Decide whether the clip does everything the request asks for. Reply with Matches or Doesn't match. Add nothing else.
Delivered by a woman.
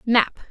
Matches